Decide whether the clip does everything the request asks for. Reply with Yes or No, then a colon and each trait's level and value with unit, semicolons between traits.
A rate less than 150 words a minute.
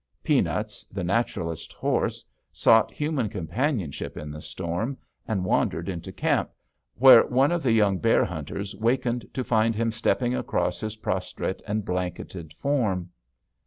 Yes: average, 140 wpm